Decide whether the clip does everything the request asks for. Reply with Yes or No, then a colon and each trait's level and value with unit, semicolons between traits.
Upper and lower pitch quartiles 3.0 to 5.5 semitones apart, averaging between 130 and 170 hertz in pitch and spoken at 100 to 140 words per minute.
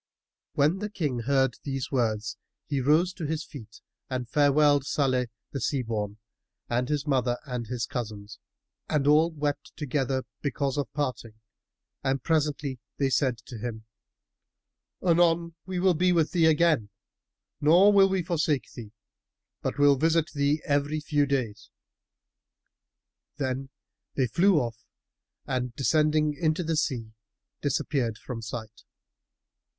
Yes: average, 3.8 semitones; medium, 140 Hz; slow, 135 wpm